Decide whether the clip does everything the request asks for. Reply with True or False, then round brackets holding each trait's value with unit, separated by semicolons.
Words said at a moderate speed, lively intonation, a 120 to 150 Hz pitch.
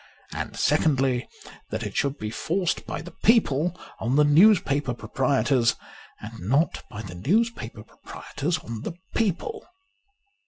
False (130 wpm; 6.5 semitones; 140 Hz)